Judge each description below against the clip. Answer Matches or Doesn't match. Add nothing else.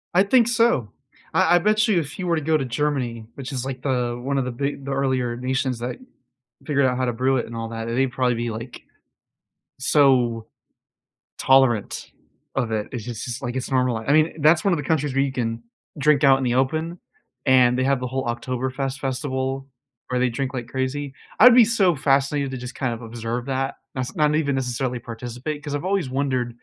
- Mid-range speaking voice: Doesn't match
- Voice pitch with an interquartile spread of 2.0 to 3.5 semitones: Matches